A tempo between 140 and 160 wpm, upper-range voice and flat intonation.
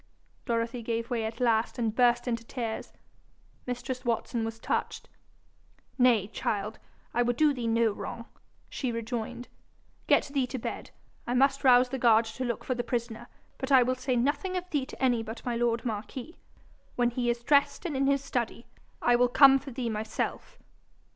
No: average, 185 wpm; high, 240 Hz; narrow, 2.0 semitones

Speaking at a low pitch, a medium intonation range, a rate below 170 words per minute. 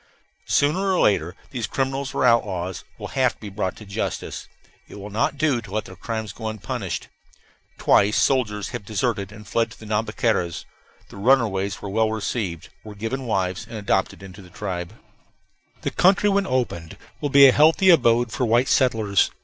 No: low, 110 Hz; average, 4.6 semitones; average, 180 wpm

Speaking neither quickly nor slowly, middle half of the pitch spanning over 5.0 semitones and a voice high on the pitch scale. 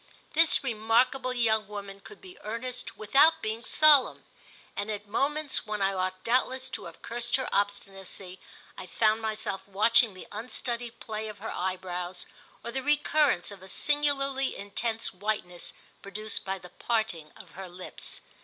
No: average, 155 wpm; average, 4.6 semitones; high, 220 Hz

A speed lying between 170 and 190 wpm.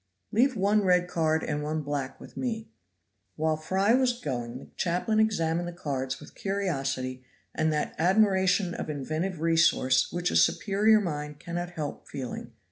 No: average, 155 wpm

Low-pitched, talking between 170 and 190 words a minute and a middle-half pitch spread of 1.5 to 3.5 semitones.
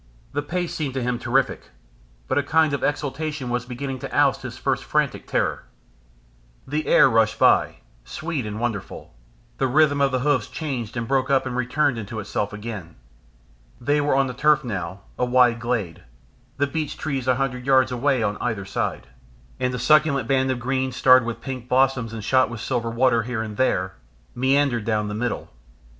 Yes: low, 130 Hz; average, 185 wpm; average, 3.1 semitones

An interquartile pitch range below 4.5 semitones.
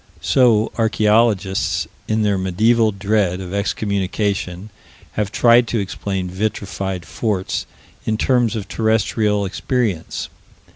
Yes: narrow, 2.6 semitones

